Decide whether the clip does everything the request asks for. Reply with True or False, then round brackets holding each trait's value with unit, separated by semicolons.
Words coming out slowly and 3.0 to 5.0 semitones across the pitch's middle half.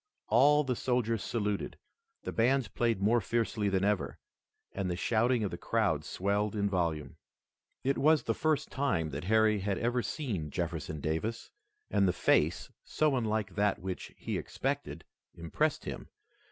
False (155 wpm; 4.3 semitones)